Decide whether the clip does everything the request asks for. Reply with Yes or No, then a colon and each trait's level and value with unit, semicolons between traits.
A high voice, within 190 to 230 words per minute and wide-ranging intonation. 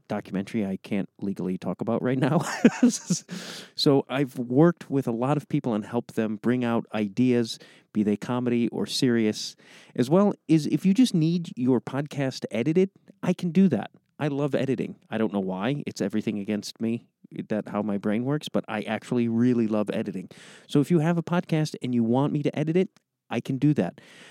No: low, 130 Hz; average, 200 wpm; wide, 6.1 semitones